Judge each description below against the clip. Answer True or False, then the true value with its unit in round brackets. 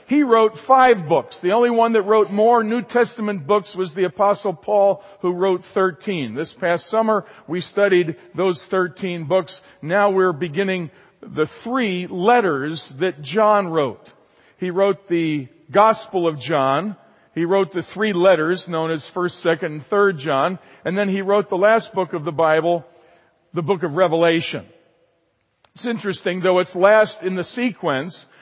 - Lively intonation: False (3.3 semitones)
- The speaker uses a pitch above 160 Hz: True (185 Hz)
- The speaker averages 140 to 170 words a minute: True (165 wpm)